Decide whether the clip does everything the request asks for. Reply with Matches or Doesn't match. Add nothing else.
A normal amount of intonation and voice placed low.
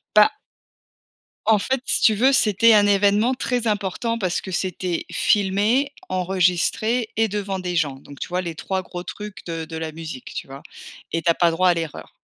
Doesn't match